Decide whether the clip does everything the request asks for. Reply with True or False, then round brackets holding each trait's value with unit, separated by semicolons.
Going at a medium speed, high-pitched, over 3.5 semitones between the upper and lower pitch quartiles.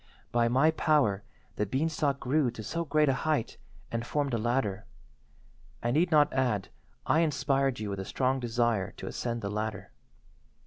False (170 wpm; 125 Hz; 4.8 semitones)